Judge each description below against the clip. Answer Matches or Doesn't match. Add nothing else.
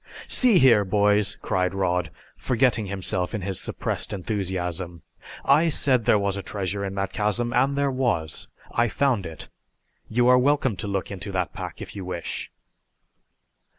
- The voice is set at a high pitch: Doesn't match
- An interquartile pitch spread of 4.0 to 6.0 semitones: Matches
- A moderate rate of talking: Matches